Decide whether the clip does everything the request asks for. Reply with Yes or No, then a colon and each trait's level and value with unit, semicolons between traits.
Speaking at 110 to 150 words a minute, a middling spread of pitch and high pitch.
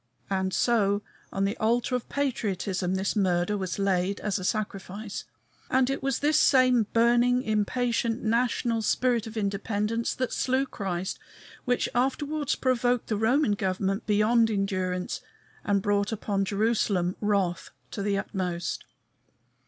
Yes: slow, 135 wpm; average, 3.6 semitones; high, 210 Hz